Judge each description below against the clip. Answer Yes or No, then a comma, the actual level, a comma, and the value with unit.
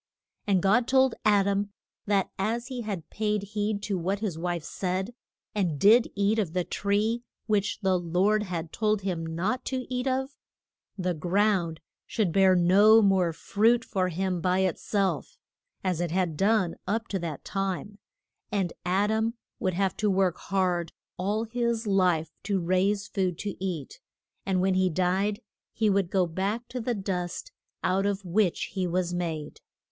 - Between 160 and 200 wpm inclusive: Yes, average, 170 wpm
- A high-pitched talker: Yes, high, 195 Hz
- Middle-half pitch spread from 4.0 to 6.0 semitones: No, average, 2.8 semitones